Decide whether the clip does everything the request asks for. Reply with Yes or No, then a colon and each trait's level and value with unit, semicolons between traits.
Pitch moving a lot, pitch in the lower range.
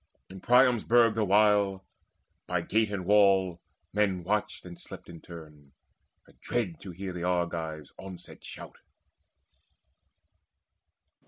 No: average, 3.4 semitones; very low, 95 Hz